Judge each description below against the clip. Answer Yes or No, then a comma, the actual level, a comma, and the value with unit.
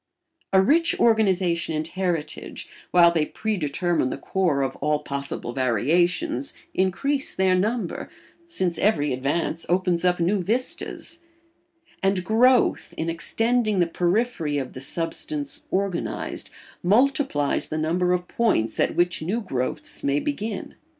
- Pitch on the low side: No, medium, 180 Hz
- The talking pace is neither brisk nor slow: No, slow, 130 wpm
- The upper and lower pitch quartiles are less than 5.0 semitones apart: No, wide, 5.6 semitones